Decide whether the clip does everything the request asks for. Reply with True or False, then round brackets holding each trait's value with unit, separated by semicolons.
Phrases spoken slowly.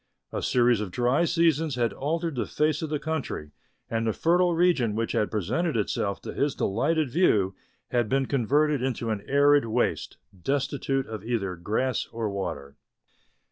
False (165 wpm)